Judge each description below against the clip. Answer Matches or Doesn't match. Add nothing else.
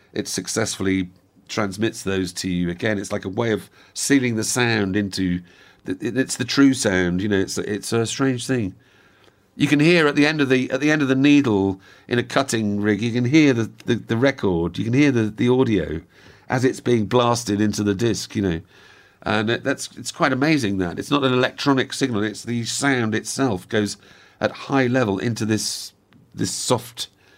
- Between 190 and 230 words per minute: Matches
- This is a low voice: Matches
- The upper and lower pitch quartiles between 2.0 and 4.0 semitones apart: Doesn't match